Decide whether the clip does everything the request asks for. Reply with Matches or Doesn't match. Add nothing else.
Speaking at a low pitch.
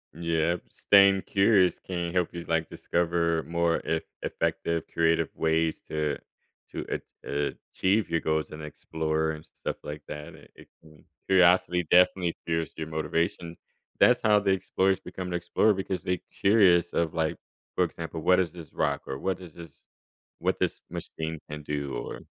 Matches